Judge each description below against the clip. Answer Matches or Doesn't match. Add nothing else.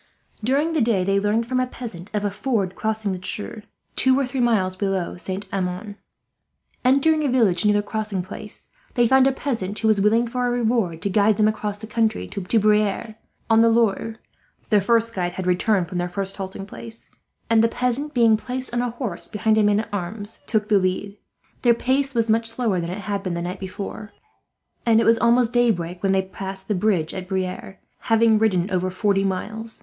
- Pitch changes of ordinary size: Matches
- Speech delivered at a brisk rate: Matches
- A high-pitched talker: Matches